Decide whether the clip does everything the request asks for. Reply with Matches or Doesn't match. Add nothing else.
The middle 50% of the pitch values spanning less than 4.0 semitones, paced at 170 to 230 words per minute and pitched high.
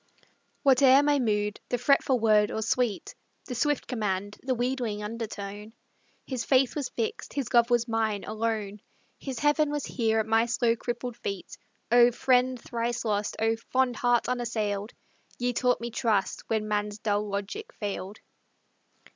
Doesn't match